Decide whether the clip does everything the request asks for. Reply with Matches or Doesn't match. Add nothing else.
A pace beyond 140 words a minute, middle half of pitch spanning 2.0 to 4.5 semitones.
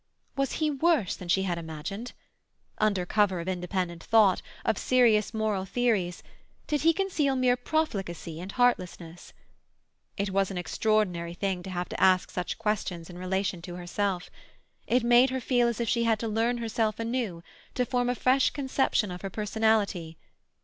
Doesn't match